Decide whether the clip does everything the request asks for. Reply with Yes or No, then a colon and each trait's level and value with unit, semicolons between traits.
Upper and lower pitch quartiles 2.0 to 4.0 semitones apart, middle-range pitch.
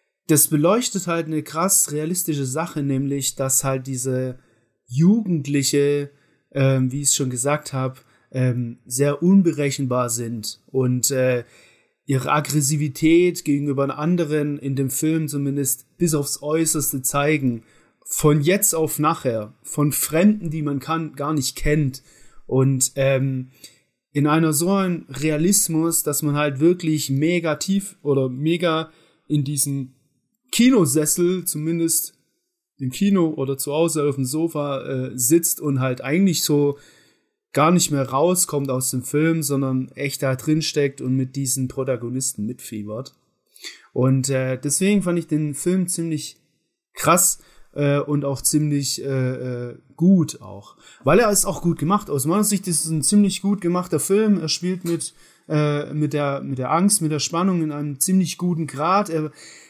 Yes: average, 3.6 semitones; medium, 150 Hz